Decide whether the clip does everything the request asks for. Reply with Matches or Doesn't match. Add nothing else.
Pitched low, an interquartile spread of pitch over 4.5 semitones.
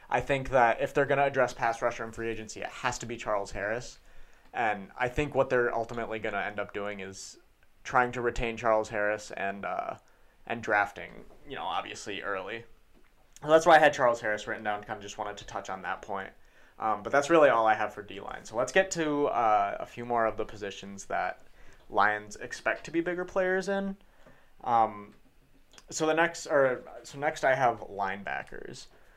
Matches